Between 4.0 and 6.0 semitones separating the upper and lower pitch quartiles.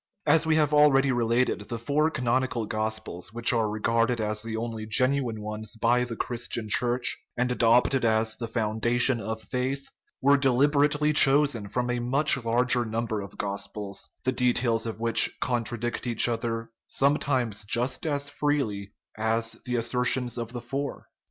No: average, 2.7 semitones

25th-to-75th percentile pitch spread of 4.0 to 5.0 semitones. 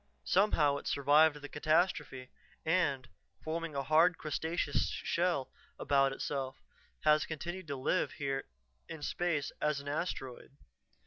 No: average, 2.9 semitones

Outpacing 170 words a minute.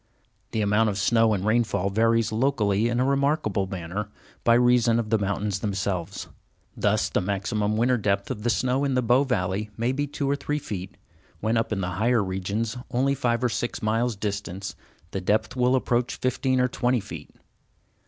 Yes: average, 185 wpm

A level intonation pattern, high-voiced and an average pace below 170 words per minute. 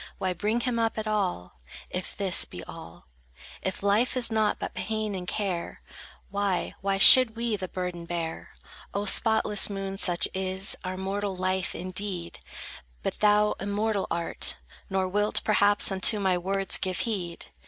Yes: narrow, 2.3 semitones; high, 195 Hz; average, 155 wpm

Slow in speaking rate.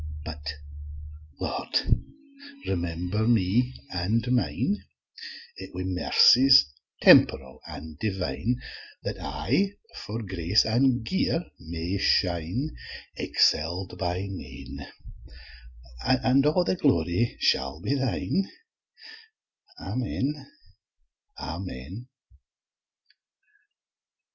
Yes: slow, 75 wpm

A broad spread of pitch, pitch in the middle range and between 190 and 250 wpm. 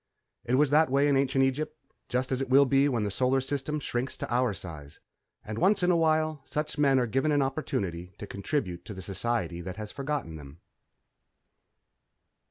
No: wide, 5.7 semitones; low, 130 Hz; average, 195 wpm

